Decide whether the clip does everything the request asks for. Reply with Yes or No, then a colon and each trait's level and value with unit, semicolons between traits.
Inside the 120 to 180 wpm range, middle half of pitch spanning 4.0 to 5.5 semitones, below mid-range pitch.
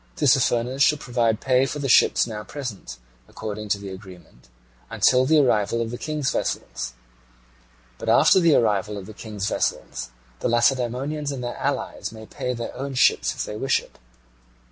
Yes: average, 170 wpm; average, 4.3 semitones; low, 120 Hz